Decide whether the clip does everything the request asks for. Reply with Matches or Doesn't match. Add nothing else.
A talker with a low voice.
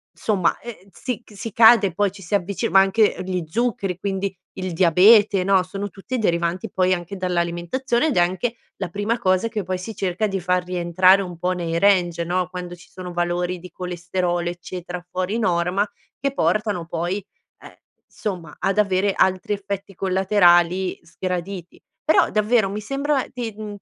Doesn't match